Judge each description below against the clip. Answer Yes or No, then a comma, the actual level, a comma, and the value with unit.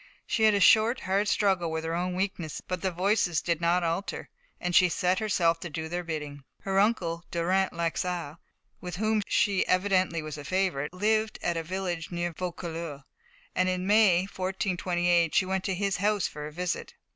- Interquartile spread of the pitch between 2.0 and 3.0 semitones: Yes, narrow, 2.4 semitones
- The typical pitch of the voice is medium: Yes, medium, 180 Hz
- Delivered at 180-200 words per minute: Yes, average, 185 wpm